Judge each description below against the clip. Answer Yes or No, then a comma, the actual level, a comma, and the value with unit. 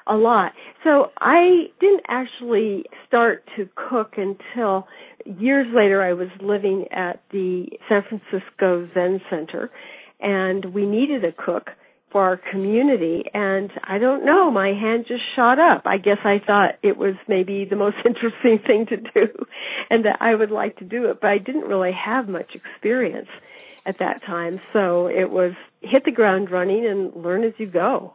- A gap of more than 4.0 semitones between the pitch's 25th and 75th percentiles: No, average, 3.7 semitones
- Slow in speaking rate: No, average, 175 wpm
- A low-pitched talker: No, high, 205 Hz